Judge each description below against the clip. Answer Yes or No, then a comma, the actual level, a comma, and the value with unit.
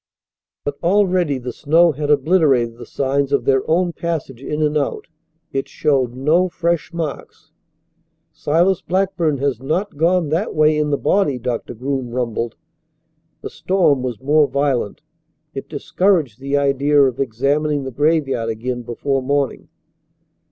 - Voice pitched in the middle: Yes, medium, 145 Hz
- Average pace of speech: Yes, average, 145 wpm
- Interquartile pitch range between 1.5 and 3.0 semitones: No, average, 3.7 semitones